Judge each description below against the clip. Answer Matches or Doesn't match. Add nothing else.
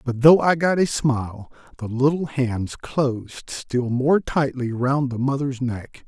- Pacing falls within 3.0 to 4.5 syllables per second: Matches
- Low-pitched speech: Matches